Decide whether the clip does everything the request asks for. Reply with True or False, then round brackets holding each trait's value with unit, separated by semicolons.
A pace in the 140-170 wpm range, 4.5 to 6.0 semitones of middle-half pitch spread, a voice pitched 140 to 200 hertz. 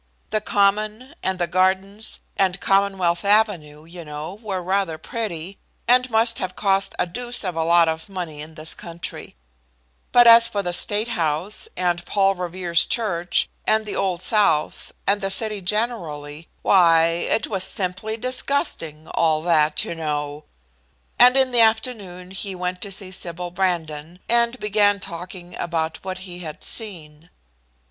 False (155 wpm; 3.9 semitones; 185 Hz)